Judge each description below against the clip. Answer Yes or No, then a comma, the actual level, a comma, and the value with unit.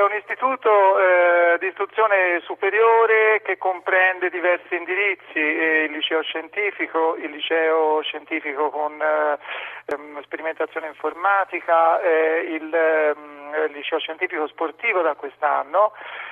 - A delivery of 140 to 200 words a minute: No, slow, 115 wpm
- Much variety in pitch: No, average, 3.6 semitones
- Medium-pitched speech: Yes, medium, 165 Hz